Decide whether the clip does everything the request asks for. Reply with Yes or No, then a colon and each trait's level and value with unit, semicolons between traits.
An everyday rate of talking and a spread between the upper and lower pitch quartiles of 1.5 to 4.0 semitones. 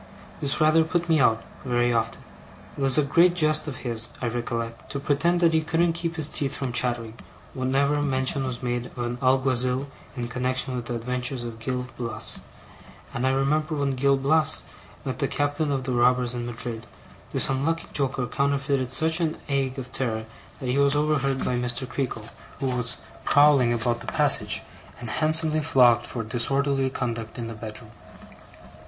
Yes: average, 180 wpm; average, 3.0 semitones